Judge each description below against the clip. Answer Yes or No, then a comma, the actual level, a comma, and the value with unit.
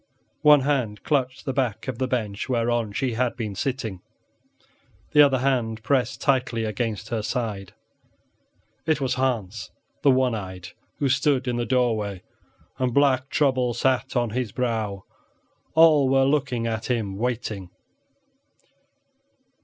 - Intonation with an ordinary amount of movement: Yes, average, 3.2 semitones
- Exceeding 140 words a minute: No, slow, 135 wpm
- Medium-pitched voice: No, low, 125 Hz